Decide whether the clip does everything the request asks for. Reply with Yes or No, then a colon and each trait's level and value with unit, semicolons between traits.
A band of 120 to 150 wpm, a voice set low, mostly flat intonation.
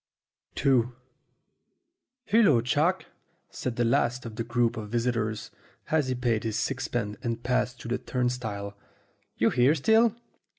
Yes: average, 140 wpm; low, 120 Hz; narrow, 2.1 semitones